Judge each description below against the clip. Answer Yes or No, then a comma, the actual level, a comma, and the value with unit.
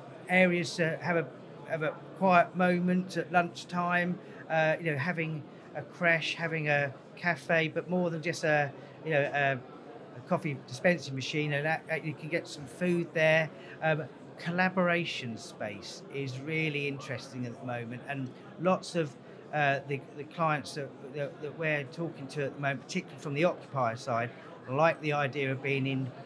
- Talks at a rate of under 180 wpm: Yes, average, 170 wpm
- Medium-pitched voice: Yes, medium, 155 Hz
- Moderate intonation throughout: Yes, average, 3.4 semitones